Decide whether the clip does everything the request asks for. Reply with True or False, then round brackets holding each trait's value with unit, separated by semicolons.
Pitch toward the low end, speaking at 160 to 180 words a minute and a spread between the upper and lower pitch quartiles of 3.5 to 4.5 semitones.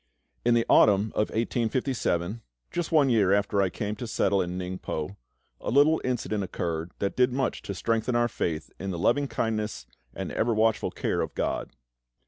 True (110 Hz; 175 wpm; 4.0 semitones)